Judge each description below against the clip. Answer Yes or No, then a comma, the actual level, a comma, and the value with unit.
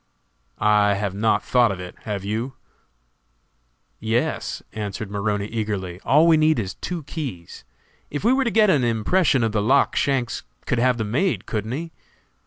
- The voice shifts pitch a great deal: Yes, wide, 5.7 semitones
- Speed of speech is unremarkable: Yes, average, 170 wpm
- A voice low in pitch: Yes, low, 115 Hz